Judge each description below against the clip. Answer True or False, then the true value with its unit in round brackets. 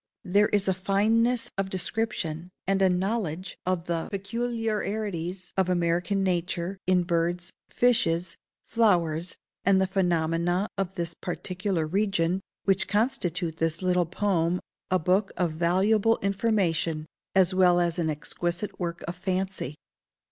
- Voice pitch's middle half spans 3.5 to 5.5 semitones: False (2.5 semitones)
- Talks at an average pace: False (130 wpm)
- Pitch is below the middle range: False (185 Hz)